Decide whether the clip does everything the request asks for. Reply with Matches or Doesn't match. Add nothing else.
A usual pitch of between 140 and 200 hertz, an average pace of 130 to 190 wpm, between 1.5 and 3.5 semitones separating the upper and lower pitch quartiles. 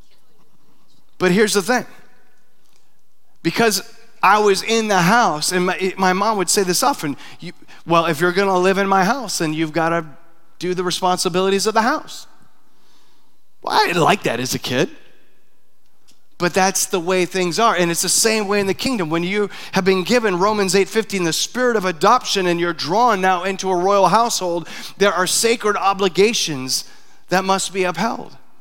Matches